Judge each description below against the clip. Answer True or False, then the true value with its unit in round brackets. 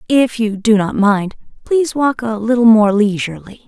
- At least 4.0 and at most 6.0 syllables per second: True (5.0 syllables/s)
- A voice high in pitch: True (220 Hz)